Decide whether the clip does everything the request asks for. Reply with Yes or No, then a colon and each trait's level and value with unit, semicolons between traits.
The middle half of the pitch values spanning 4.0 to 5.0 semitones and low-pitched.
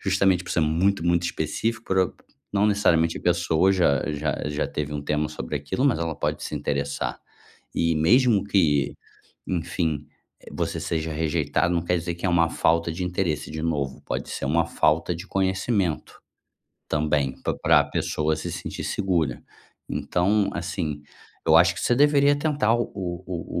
No: average, 3.6 semitones; very low, 85 Hz